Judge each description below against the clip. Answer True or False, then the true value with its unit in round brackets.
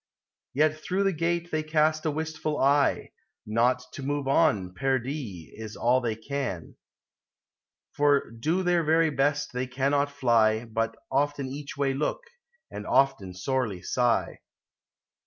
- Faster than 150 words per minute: False (140 wpm)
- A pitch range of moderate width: True (4.5 semitones)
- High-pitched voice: False (140 Hz)